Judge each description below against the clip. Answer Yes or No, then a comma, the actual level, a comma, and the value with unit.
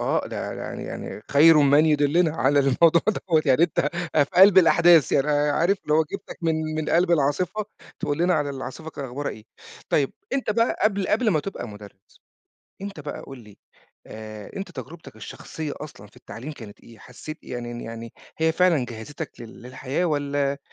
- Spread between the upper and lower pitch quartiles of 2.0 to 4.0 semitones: No, average, 4.4 semitones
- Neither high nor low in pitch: Yes, medium, 150 Hz